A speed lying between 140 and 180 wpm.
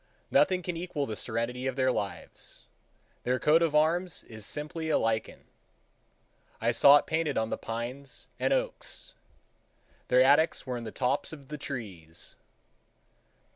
Yes: average, 150 wpm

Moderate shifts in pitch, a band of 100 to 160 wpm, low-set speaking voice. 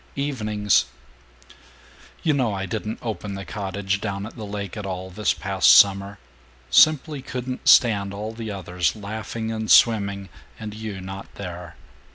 No: narrow, 2.2 semitones; average, 150 wpm; low, 105 Hz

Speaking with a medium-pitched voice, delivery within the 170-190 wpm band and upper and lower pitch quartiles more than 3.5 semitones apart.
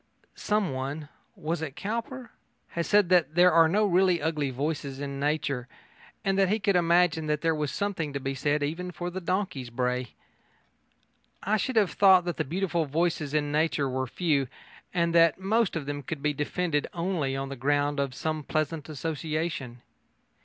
Yes: medium, 160 Hz; average, 175 wpm; average, 4.0 semitones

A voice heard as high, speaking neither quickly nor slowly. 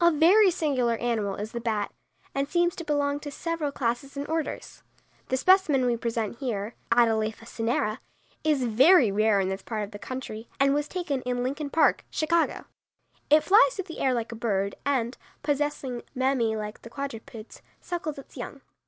Yes: very high, 260 Hz; average, 180 wpm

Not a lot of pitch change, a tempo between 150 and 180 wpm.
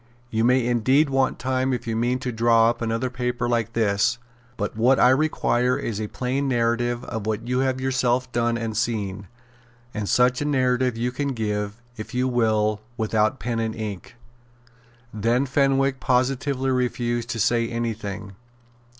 Yes: narrow, 2.3 semitones; average, 165 wpm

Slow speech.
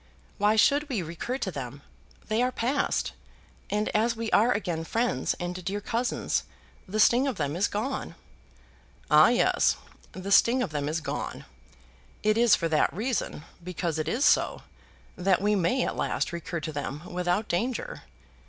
No: average, 165 wpm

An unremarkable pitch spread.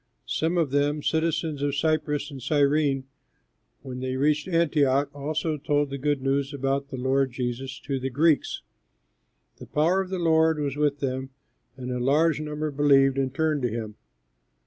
No: narrow, 2.3 semitones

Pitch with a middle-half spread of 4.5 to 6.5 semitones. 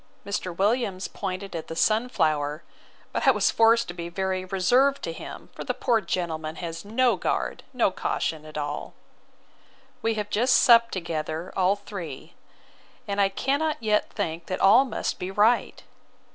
Yes: average, 5.1 semitones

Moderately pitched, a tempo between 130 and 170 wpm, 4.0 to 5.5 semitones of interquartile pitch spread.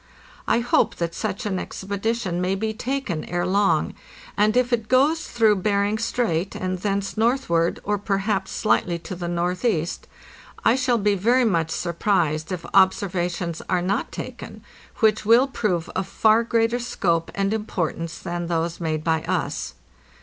No: high, 195 Hz; average, 155 wpm; average, 4.3 semitones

